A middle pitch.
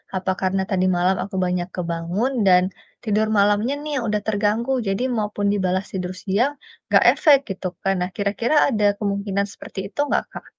No: high, 200 Hz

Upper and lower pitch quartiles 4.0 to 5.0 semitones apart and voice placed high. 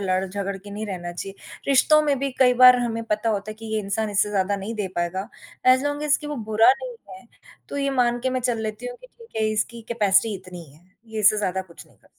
Yes: average, 4.5 semitones; high, 215 Hz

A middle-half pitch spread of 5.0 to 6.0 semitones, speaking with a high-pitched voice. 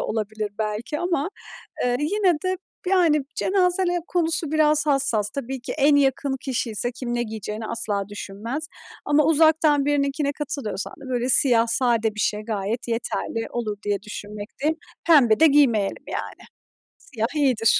Yes: wide, 5.4 semitones; very high, 255 Hz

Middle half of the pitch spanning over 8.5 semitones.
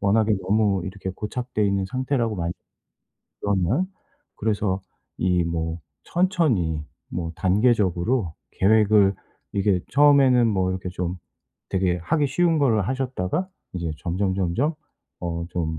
No: wide, 5.5 semitones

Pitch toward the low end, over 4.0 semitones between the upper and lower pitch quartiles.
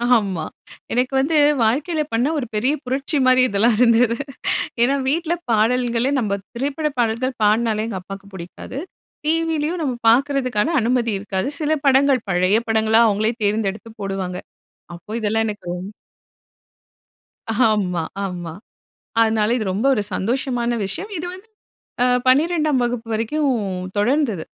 No: high, 235 Hz; average, 4.6 semitones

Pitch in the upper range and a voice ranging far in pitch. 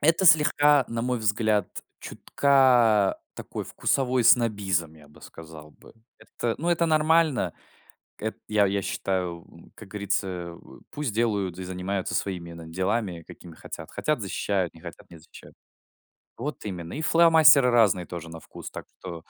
No: low, 100 Hz; wide, 6.3 semitones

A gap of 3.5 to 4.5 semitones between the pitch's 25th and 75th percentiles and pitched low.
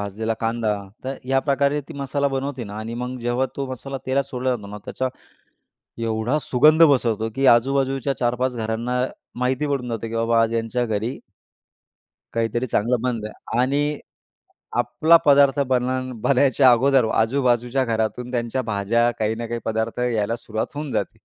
No: average, 2.9 semitones; low, 125 Hz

